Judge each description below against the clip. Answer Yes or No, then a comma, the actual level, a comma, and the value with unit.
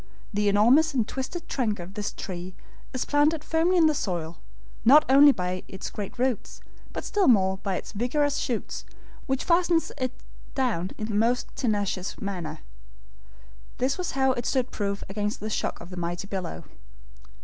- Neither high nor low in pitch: No, high, 225 Hz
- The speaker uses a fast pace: No, average, 170 wpm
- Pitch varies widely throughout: Yes, wide, 6.1 semitones